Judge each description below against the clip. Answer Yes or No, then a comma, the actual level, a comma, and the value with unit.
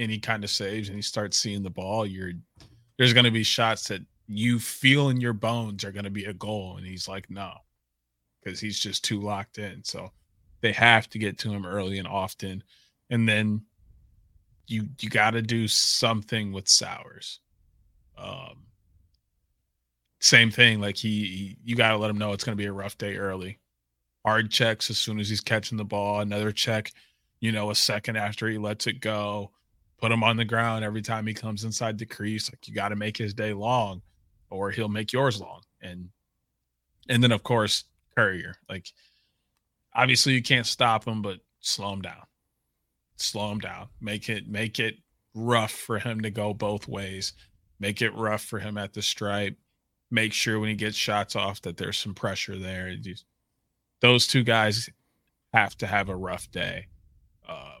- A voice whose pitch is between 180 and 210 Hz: No, low, 105 Hz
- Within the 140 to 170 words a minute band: No, average, 185 wpm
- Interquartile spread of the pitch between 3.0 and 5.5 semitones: No, narrow, 2.5 semitones